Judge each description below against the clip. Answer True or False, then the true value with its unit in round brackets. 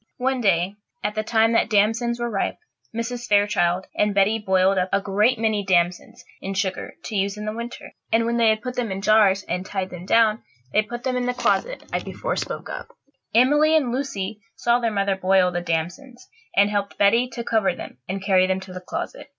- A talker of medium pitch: False (210 Hz)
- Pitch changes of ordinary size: True (3.6 semitones)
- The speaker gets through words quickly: True (215 wpm)